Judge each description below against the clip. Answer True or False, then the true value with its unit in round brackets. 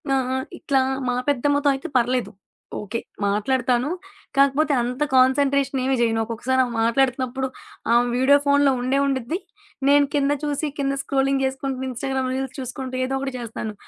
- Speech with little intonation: True (1.9 semitones)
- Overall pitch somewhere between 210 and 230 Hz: False (265 Hz)